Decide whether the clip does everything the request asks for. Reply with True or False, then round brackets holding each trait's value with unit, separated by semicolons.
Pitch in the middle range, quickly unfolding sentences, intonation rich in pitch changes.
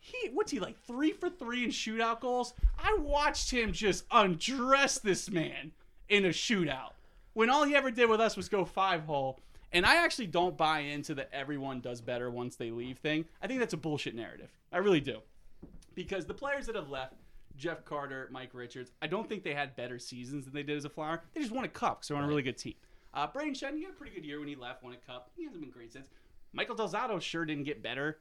True (175 Hz; 245 wpm; 9.0 semitones)